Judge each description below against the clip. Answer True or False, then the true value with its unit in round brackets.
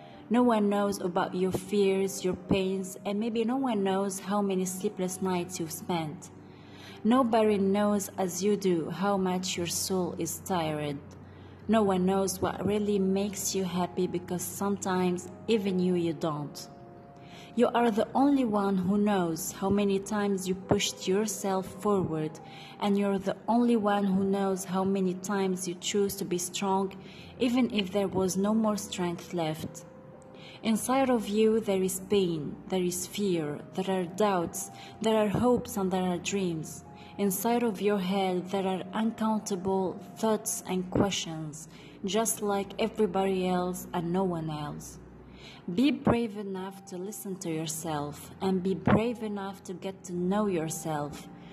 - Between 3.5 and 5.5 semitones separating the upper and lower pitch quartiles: False (2.4 semitones)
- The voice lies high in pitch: True (195 Hz)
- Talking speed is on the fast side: False (155 wpm)